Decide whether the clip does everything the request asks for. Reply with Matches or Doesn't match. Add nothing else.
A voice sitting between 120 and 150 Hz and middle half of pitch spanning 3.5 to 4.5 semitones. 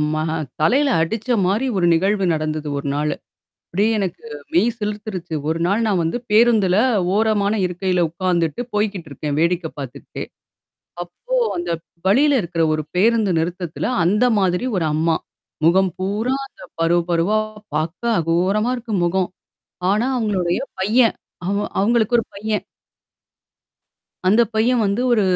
Doesn't match